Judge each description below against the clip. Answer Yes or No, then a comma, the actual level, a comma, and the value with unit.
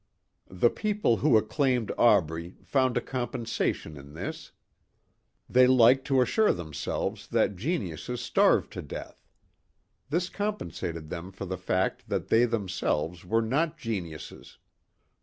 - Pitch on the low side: Yes, low, 115 Hz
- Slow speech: Yes, slow, 125 wpm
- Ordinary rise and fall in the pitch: No, wide, 6.7 semitones